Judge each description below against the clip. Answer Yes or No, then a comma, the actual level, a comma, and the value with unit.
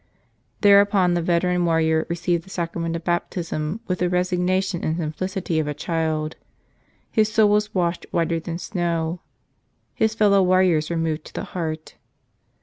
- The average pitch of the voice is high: No, medium, 175 Hz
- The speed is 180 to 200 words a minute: No, average, 155 wpm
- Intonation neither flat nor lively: No, narrow, 2.3 semitones